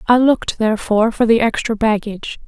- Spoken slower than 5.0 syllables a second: No, 6.1 syllables/s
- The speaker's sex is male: No, female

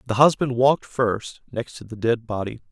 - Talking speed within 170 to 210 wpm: Yes, average, 200 wpm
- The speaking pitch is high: No, low, 120 Hz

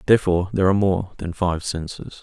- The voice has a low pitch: Yes, very low, 90 Hz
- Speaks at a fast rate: No, average, 190 wpm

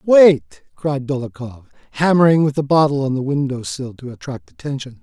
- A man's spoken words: Yes, male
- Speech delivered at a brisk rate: No, average, 165 wpm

